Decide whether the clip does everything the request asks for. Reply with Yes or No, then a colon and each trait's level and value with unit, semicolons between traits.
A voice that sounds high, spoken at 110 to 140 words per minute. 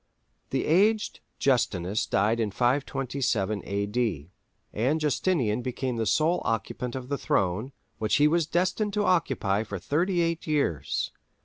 No: low, 130 Hz; slow, 135 wpm